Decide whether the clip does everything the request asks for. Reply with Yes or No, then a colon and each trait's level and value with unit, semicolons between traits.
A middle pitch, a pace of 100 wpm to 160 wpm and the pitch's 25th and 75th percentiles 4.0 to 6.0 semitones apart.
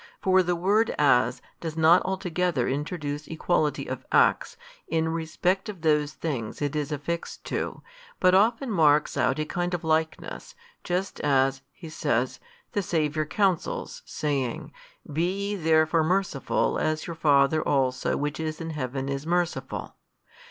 No: medium, 160 Hz; average, 145 wpm; average, 3.4 semitones